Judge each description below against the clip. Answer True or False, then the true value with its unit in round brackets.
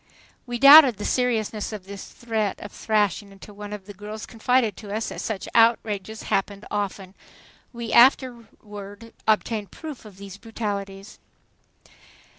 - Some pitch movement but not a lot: False (2.3 semitones)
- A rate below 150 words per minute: True (140 wpm)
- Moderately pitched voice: False (210 Hz)